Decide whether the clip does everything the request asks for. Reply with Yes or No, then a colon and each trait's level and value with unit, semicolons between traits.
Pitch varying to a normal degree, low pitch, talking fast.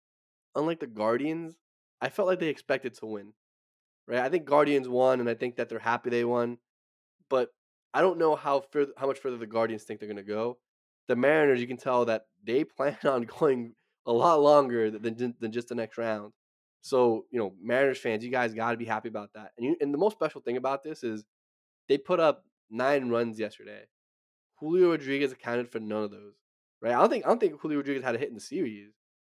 Yes: average, 4.4 semitones; low, 120 Hz; fast, 225 wpm